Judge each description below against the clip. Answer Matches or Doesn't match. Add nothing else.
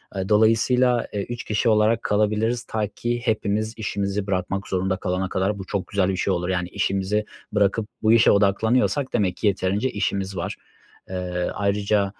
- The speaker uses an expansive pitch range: Doesn't match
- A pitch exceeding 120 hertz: Doesn't match